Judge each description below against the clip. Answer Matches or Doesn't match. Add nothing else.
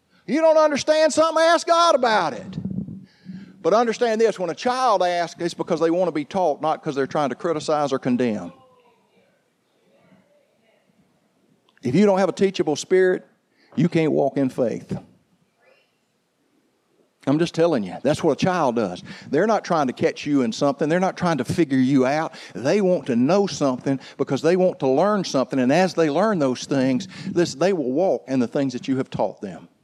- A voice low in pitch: Doesn't match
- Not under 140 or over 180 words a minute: Doesn't match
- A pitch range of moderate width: Doesn't match